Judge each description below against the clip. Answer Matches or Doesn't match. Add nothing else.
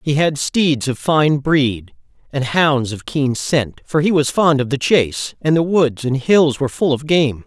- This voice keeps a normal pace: Doesn't match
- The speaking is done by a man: Matches